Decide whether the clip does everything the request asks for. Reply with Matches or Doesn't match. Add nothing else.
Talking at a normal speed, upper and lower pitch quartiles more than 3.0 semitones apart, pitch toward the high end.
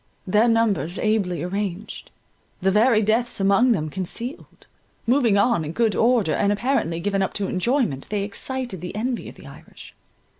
Matches